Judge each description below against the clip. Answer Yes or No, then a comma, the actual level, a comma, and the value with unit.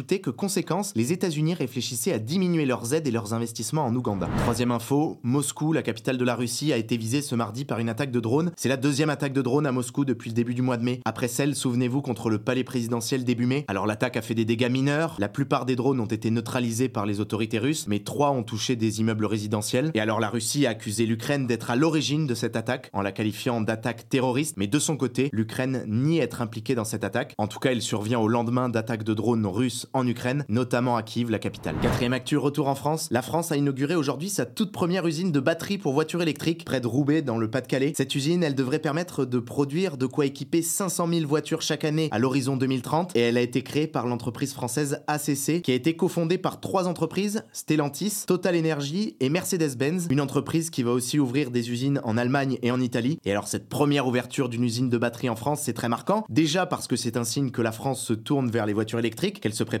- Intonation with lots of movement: No, average, 4.1 semitones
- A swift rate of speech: Yes, fast, 240 wpm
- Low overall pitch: Yes, low, 130 Hz